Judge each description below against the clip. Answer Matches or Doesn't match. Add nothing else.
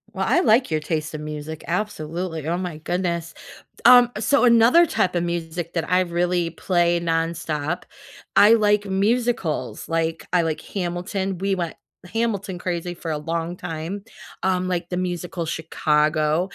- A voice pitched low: Doesn't match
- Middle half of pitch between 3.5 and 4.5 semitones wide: Doesn't match